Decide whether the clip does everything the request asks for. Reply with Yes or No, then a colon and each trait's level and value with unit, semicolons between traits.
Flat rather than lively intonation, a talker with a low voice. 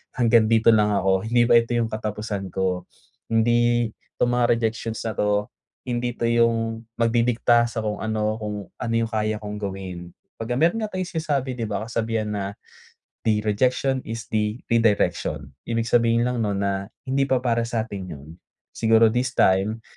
Yes: narrow, 2.0 semitones; low, 115 Hz